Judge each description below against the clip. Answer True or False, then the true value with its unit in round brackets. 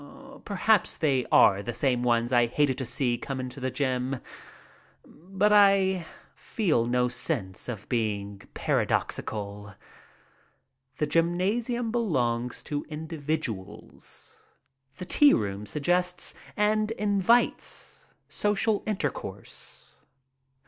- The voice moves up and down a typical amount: False (8.3 semitones)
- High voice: False (145 Hz)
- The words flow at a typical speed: False (105 wpm)